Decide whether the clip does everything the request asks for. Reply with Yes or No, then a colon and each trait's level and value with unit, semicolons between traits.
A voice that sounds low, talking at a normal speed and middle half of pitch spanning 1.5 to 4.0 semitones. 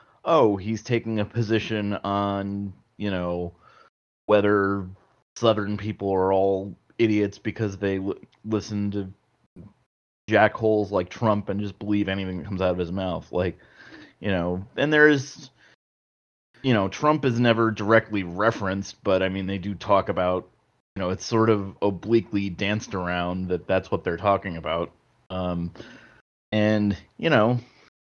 Yes: low, 100 Hz; average, 150 wpm; narrow, 2.4 semitones